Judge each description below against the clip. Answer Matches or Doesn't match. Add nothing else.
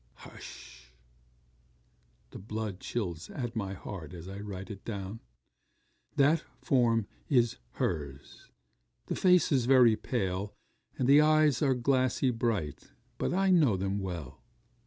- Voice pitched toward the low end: Matches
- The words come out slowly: Matches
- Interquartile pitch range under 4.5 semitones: Doesn't match